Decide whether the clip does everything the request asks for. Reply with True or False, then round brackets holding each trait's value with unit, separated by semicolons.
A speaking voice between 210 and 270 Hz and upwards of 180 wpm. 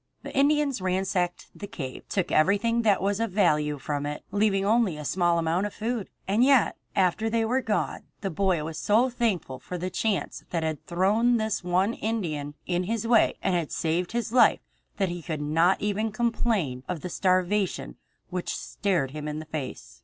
False (190 Hz; 190 wpm)